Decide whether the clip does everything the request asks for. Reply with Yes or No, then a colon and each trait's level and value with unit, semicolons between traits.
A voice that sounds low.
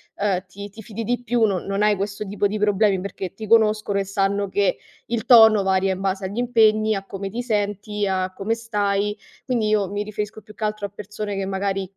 No: high, 205 Hz